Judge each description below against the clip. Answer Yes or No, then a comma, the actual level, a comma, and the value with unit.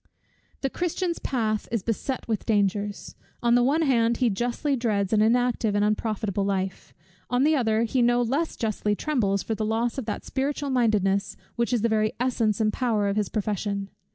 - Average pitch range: Yes, average, 3.0 semitones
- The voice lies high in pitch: Yes, high, 225 Hz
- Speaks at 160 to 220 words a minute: Yes, average, 185 wpm